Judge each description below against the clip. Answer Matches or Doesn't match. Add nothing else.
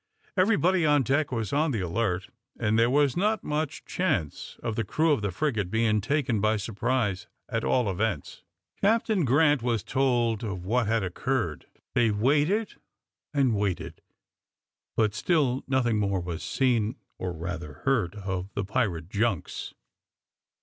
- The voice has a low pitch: Matches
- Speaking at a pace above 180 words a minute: Doesn't match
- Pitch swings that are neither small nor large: Doesn't match